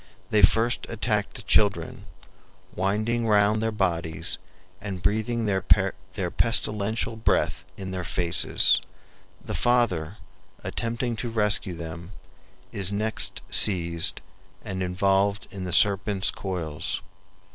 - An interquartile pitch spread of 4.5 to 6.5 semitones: No, average, 3.0 semitones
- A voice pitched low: Yes, low, 100 Hz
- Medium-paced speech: No, slow, 110 wpm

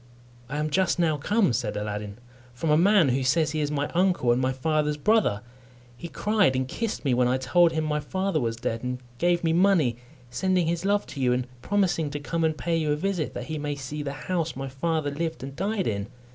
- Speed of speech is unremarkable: No, fast, 230 wpm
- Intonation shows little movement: No, average, 4.9 semitones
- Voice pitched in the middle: Yes, medium, 150 Hz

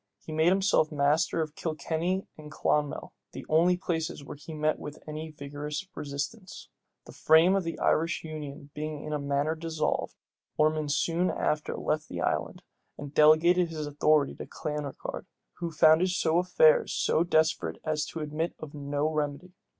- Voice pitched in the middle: Yes, medium, 155 Hz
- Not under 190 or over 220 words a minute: No, average, 160 wpm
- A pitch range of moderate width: No, narrow, 1.9 semitones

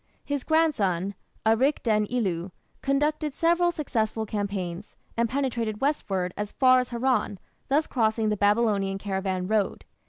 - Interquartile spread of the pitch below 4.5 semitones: No, average, 5.2 semitones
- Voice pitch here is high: Yes, high, 220 Hz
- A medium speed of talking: No, slow, 130 wpm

